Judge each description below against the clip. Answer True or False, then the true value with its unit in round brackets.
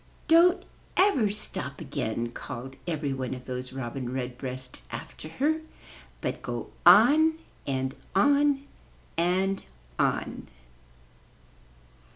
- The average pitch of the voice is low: False (145 Hz)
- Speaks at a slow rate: True (110 wpm)